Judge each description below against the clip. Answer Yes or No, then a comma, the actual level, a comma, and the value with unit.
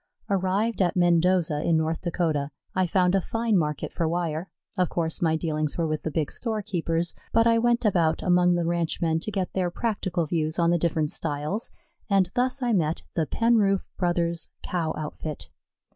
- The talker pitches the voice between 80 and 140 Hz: No, medium, 175 Hz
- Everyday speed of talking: Yes, average, 175 wpm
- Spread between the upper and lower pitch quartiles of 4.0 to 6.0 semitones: No, average, 3.3 semitones